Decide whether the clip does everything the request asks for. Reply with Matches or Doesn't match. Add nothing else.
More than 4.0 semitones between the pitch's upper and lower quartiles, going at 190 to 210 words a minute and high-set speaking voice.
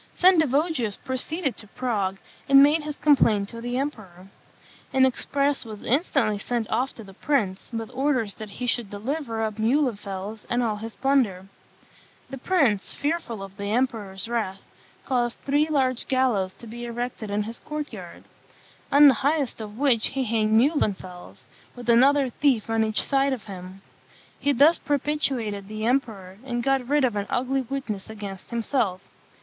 Doesn't match